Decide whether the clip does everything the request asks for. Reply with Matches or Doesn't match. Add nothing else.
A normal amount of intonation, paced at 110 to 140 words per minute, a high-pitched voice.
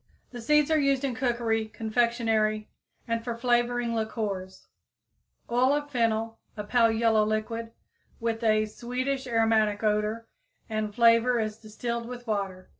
Doesn't match